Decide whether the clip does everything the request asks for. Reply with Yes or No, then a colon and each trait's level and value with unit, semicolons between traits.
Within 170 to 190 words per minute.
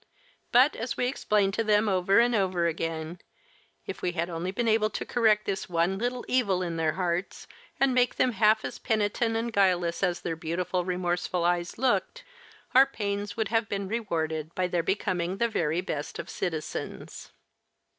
Yes: average, 175 wpm